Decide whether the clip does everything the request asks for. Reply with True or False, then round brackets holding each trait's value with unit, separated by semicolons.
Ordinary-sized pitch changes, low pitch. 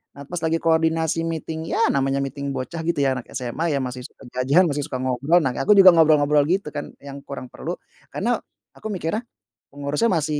False (3.2 semitones; 150 Hz)